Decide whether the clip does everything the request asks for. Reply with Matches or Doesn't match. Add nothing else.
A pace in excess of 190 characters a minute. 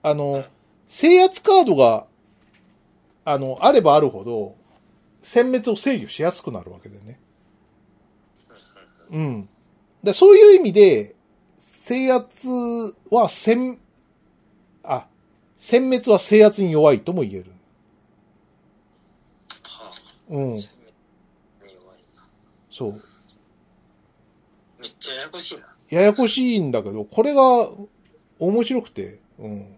Doesn't match